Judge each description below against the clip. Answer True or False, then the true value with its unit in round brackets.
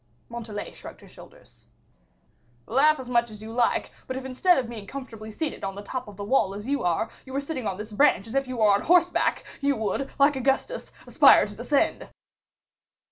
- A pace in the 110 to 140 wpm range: False (205 wpm)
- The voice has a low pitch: False (245 Hz)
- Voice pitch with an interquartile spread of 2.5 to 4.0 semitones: False (4.4 semitones)